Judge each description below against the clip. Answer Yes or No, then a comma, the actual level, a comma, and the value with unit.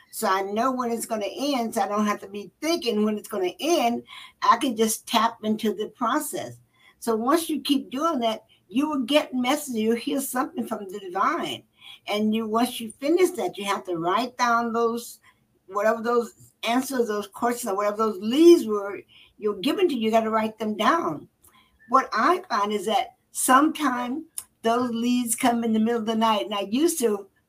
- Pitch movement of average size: Yes, average, 3.9 semitones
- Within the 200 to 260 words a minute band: Yes, fast, 205 wpm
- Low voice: No, high, 230 Hz